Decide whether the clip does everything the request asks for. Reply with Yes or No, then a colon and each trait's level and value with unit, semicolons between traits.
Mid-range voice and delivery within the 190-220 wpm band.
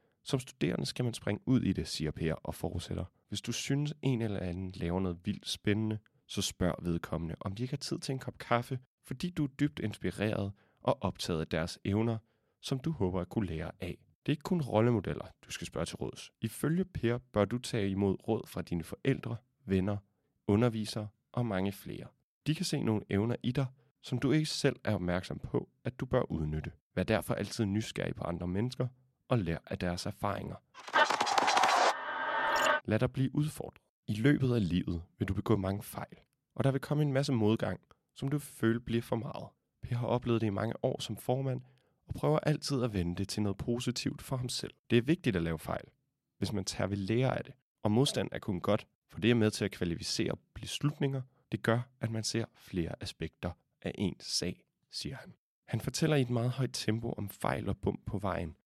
No: low, 115 Hz; average, 210 wpm